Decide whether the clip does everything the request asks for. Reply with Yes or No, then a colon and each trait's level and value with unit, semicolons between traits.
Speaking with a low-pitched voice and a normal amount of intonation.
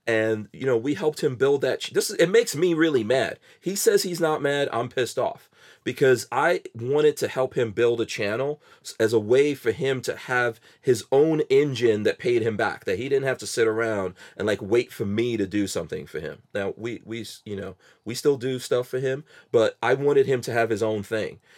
No: low, 130 Hz; wide, 7.4 semitones